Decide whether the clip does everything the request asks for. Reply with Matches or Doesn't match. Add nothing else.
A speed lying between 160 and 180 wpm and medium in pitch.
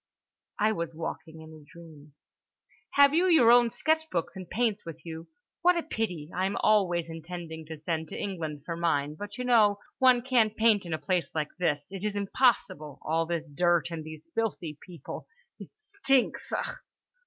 Matches